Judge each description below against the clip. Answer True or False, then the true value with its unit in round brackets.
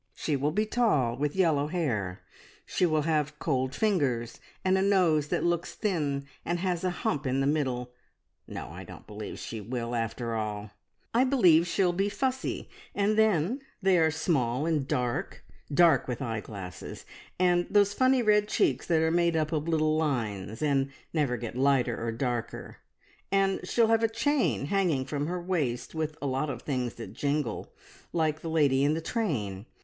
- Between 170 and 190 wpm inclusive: True (175 wpm)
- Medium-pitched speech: True (150 Hz)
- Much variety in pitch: True (6.1 semitones)